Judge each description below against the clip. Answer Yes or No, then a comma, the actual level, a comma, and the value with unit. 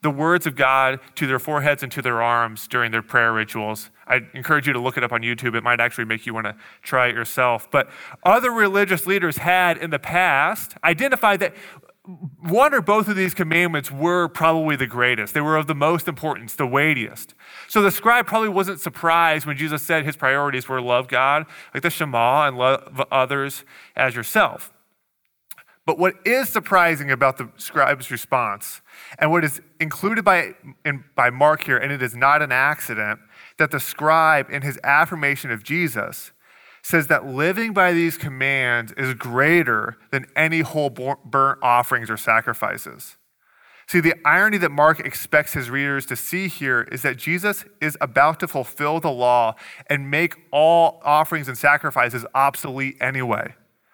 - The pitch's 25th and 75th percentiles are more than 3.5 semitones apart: Yes, average, 4.5 semitones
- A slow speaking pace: No, average, 175 wpm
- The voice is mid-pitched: Yes, medium, 145 Hz